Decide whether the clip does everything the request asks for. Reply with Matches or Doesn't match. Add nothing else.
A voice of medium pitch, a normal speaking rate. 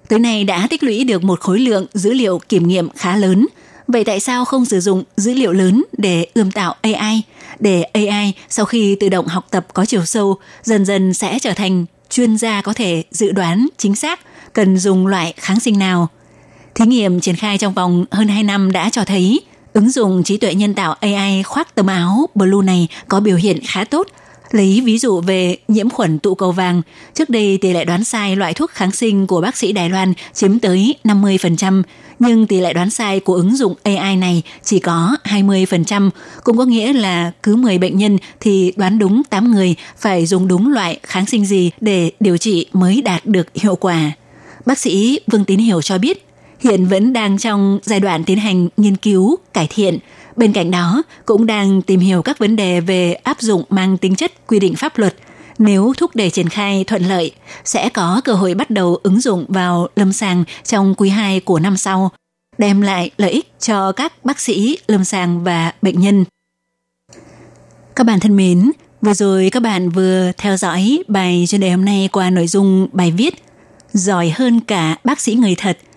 Doesn't match